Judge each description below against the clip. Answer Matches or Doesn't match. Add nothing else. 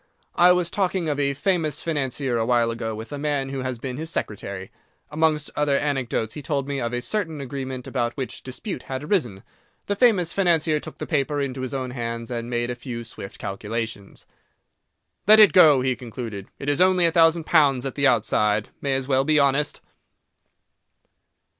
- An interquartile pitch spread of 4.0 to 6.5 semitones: Matches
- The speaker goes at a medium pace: Matches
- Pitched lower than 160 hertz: Matches